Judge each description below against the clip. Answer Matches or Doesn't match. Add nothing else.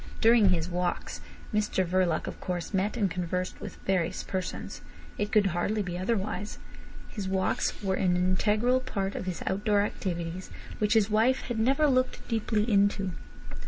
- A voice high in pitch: Matches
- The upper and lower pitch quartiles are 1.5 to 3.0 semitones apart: Matches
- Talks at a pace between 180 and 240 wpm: Doesn't match